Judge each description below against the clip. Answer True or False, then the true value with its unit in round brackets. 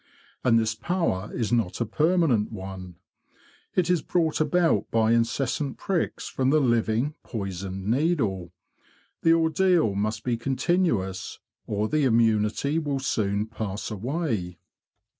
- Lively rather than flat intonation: True (6.7 semitones)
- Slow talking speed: True (125 wpm)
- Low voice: True (115 Hz)